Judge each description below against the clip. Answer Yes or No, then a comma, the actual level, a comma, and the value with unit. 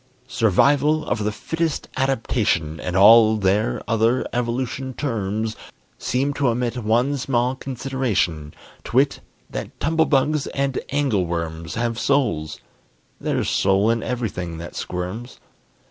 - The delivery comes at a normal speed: No, slow, 115 wpm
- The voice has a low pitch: Yes, low, 115 Hz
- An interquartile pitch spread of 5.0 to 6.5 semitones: Yes, wide, 5.4 semitones